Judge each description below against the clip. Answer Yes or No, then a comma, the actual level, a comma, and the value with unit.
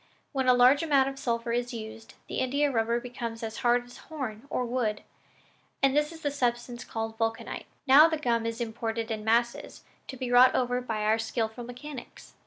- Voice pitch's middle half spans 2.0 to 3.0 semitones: Yes, narrow, 2.6 semitones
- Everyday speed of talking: Yes, average, 195 wpm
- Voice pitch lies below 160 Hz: No, high, 245 Hz